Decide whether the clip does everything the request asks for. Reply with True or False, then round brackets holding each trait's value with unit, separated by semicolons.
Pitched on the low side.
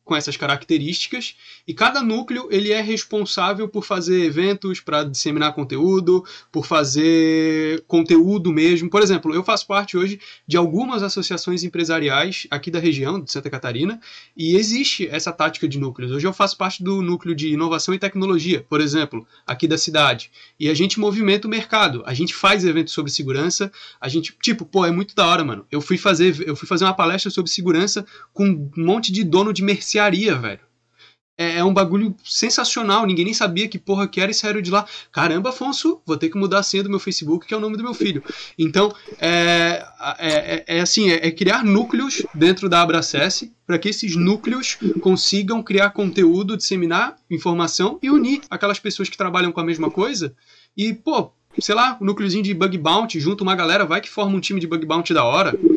False (185 Hz)